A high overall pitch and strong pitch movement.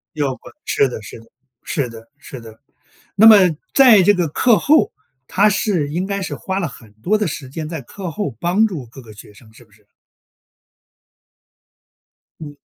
No: medium, 155 Hz; wide, 8.5 semitones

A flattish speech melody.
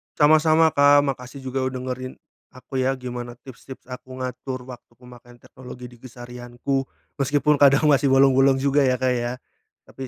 Yes: narrow, 1.6 semitones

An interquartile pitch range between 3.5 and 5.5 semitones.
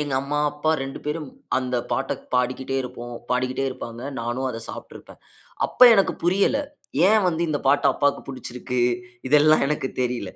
No: average, 2.9 semitones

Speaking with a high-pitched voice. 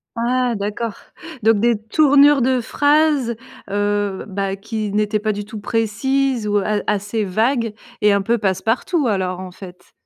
Yes: high, 215 Hz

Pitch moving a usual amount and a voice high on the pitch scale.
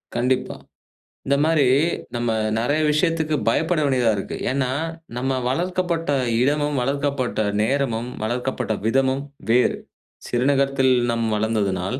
No: average, 3.4 semitones; low, 130 Hz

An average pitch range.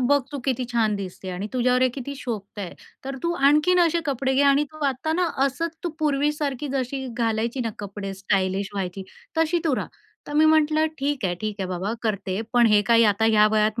No: wide, 5.8 semitones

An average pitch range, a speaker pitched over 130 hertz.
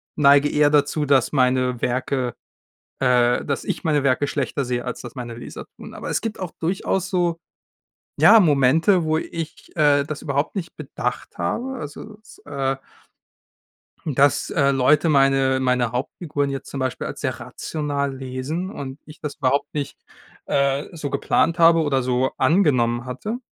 Yes: average, 3.3 semitones; medium, 140 Hz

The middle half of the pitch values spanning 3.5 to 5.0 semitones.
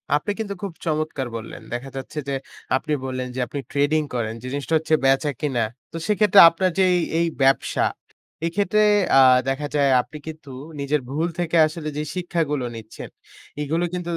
Yes: average, 3.9 semitones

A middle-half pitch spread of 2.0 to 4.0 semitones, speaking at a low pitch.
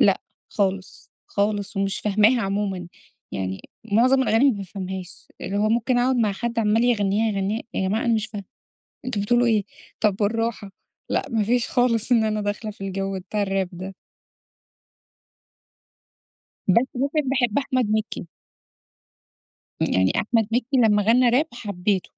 No: average, 3.3 semitones; high, 215 Hz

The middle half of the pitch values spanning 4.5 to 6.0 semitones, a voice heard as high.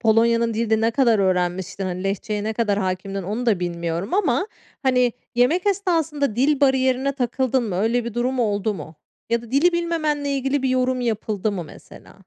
Yes: average, 4.8 semitones; high, 235 Hz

